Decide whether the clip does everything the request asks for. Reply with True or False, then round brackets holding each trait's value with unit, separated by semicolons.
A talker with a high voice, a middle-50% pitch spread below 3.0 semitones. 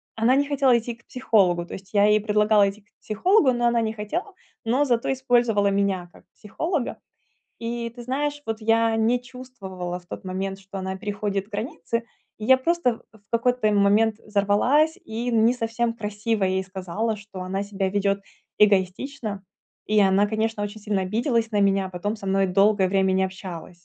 False (215 Hz; 3.4 semitones)